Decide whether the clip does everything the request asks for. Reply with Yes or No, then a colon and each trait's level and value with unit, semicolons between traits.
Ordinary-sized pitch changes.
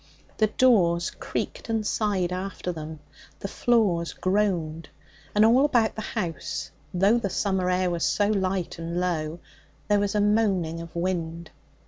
Yes: average, 3.7 semitones